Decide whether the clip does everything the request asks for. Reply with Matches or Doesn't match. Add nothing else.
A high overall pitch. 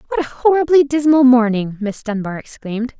Matches